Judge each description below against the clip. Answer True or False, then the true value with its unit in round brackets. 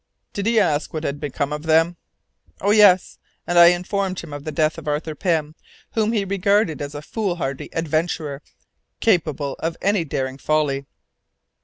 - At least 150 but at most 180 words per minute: True (165 wpm)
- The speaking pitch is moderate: True (160 Hz)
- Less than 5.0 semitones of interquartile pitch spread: True (4.2 semitones)